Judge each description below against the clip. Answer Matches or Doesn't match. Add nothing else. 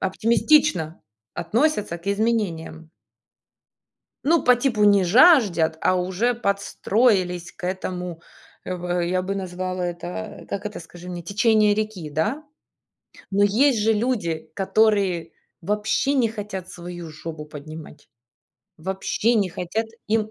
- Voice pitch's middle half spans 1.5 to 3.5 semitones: Doesn't match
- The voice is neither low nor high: Doesn't match